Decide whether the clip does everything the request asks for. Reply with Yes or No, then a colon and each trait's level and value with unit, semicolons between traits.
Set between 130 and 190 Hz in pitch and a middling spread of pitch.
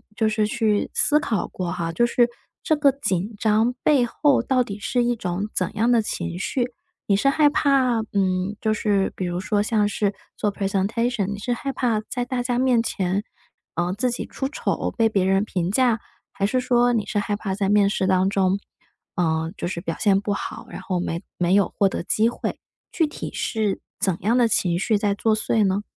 No: high, 210 Hz; average, 3.8 semitones